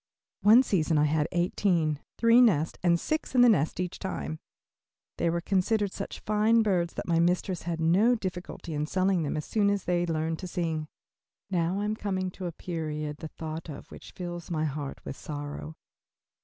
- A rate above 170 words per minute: Yes, average, 190 wpm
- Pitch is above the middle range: No, medium, 175 Hz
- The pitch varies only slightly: No, average, 3.8 semitones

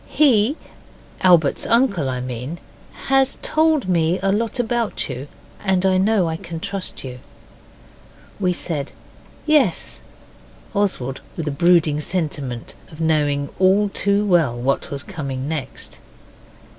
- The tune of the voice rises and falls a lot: Yes, wide, 6.1 semitones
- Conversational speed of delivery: No, slow, 130 wpm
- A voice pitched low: No, medium, 175 Hz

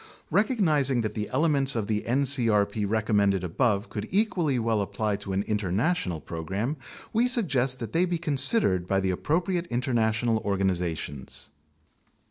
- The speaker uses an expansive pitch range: Yes, wide, 6.4 semitones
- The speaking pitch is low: Yes, low, 115 Hz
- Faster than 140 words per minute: No, slow, 135 wpm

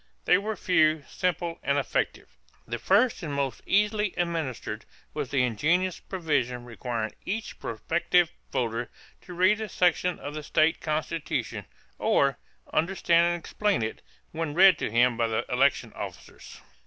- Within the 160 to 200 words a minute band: No, average, 145 wpm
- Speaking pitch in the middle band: Yes, medium, 160 Hz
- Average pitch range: No, wide, 6.3 semitones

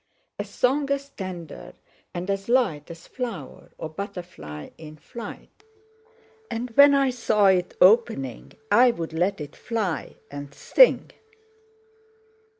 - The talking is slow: Yes, slow, 120 wpm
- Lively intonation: Yes, wide, 7.3 semitones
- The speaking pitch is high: Yes, high, 195 Hz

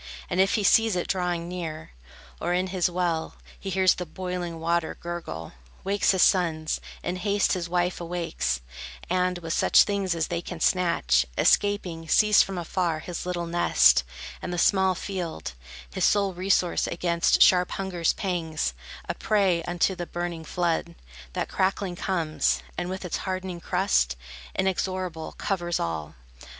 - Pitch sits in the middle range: Yes, medium, 175 Hz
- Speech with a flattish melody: Yes, narrow, 1.9 semitones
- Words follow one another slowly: No, average, 155 wpm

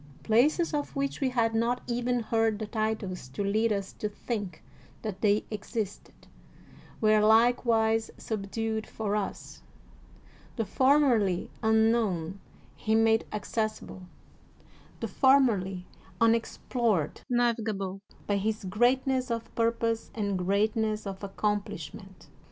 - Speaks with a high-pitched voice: Yes, high, 220 Hz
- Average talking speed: No, slow, 115 wpm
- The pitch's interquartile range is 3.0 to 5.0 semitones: No, narrow, 2.4 semitones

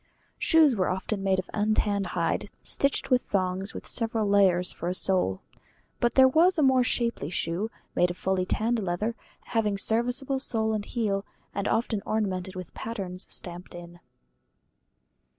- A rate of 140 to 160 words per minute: Yes, average, 155 wpm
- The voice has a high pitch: Yes, high, 205 Hz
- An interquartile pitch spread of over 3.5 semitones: Yes, average, 4.1 semitones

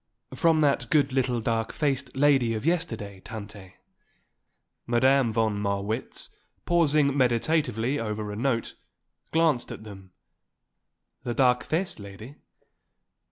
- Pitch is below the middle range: Yes, low, 120 Hz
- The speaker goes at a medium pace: No, slow, 115 wpm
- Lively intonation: No, average, 4.7 semitones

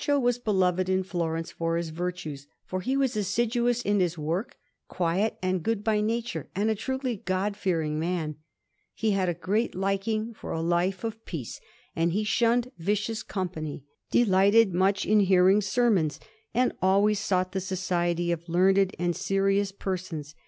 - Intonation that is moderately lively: Yes, average, 3.6 semitones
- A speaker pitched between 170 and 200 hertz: Yes, high, 190 Hz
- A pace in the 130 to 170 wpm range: Yes, average, 165 wpm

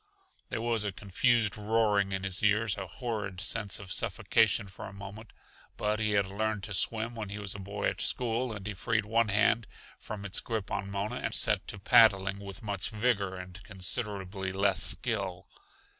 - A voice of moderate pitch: No, low, 105 Hz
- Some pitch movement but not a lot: No, narrow, 2.2 semitones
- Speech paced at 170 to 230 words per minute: Yes, average, 190 wpm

